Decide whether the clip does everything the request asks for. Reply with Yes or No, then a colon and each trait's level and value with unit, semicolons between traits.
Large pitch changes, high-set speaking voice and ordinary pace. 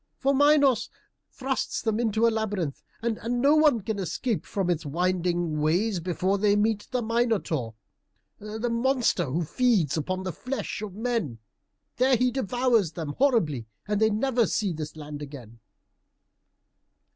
Yes: wide, 6.2 semitones; high, 210 Hz; average, 145 wpm